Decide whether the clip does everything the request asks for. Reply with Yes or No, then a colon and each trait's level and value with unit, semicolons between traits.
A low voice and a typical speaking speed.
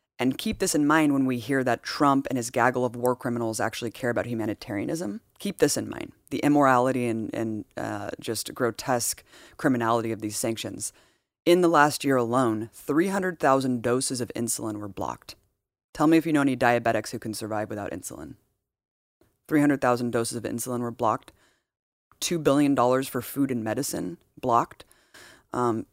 Yes: low, 125 Hz; average, 165 wpm